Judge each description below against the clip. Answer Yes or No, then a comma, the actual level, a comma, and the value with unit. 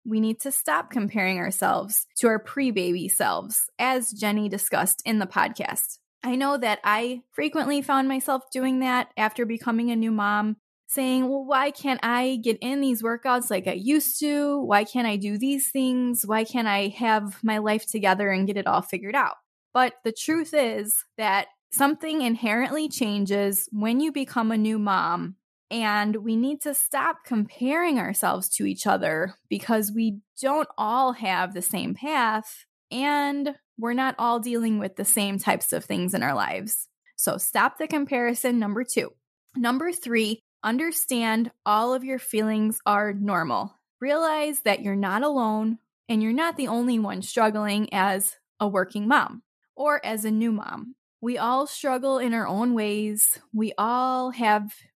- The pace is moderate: Yes, average, 170 wpm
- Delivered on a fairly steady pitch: No, average, 4.0 semitones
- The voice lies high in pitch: Yes, high, 230 Hz